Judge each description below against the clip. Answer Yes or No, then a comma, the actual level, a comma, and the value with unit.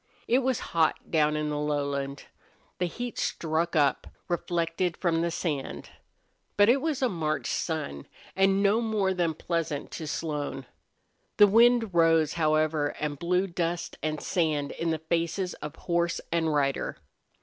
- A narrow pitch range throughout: No, average, 3.3 semitones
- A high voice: No, medium, 165 Hz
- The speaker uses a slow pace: No, average, 150 wpm